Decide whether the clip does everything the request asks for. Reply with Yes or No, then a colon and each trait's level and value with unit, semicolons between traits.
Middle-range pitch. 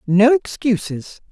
No: high, 220 Hz